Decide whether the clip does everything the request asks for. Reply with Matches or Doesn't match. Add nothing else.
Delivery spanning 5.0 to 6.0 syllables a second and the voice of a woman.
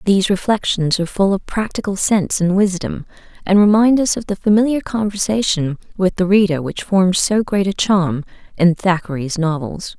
Matches